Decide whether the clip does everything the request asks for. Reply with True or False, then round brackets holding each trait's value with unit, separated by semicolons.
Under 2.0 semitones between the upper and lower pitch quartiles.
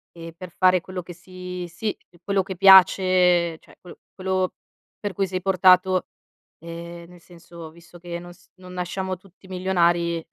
True (1.5 semitones)